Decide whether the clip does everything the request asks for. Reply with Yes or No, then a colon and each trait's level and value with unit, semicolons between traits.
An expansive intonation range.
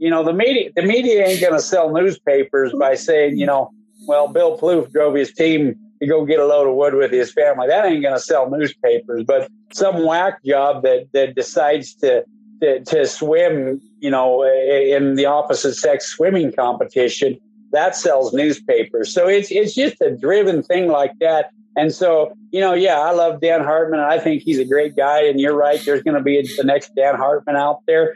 Yes: wide, 8.7 semitones